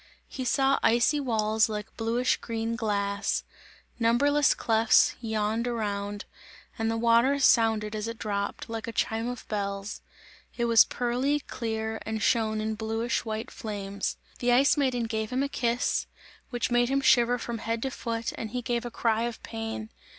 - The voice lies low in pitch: No, high, 230 Hz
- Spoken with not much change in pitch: Yes, narrow, 1.8 semitones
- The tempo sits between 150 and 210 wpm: Yes, average, 165 wpm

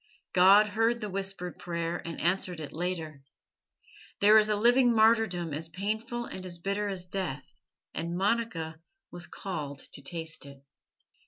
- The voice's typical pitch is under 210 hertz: Yes, medium, 185 Hz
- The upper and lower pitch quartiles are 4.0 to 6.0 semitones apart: Yes, average, 4.3 semitones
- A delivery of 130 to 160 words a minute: Yes, average, 150 wpm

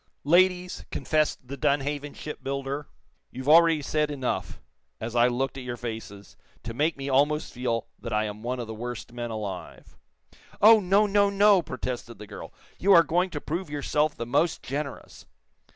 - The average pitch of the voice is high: No, medium, 140 Hz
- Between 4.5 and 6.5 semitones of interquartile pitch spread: Yes, average, 5.0 semitones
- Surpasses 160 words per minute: Yes, average, 170 wpm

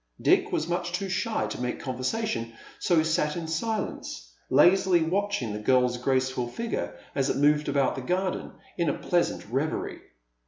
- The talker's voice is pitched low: No, medium, 150 Hz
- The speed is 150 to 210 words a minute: Yes, average, 165 wpm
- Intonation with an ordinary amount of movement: No, wide, 5.8 semitones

